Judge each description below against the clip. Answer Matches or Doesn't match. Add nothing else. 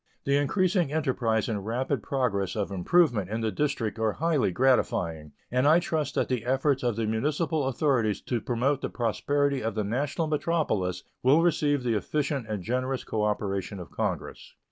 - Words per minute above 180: Doesn't match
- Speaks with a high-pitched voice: Doesn't match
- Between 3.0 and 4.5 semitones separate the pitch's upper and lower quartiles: Doesn't match